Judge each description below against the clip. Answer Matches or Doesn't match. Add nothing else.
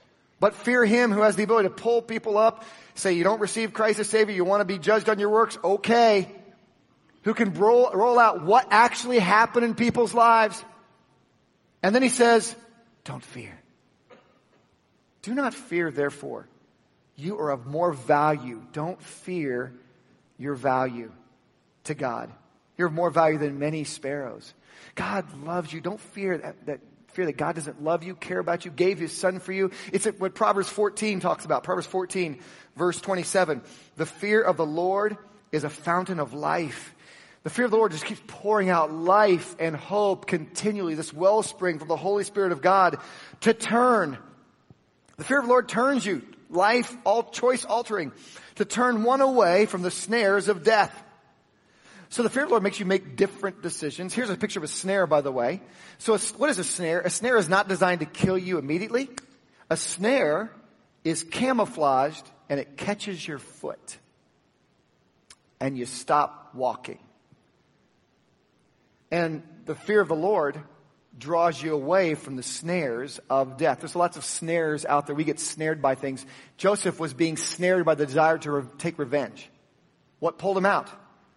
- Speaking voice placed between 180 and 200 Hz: Matches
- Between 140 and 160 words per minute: Doesn't match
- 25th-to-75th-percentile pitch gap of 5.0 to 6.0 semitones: Matches